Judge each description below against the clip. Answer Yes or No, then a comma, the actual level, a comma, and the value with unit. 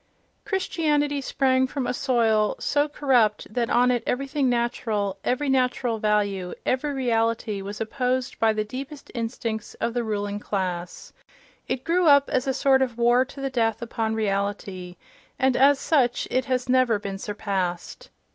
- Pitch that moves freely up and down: No, average, 3.9 semitones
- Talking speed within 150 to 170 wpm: Yes, average, 155 wpm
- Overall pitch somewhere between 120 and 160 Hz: No, high, 245 Hz